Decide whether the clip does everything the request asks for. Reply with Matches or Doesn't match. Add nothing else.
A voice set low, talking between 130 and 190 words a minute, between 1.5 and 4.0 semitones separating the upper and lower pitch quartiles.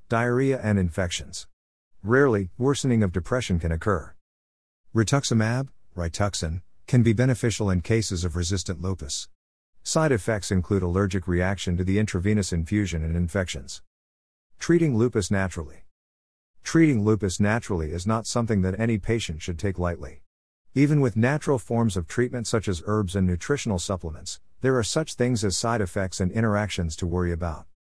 Doesn't match